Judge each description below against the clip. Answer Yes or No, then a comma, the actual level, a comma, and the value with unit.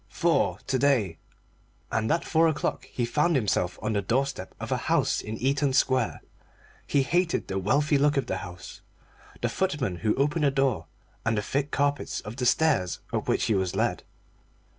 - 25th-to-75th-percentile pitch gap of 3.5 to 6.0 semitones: Yes, average, 5.3 semitones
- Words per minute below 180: No, average, 185 wpm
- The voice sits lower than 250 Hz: Yes, low, 135 Hz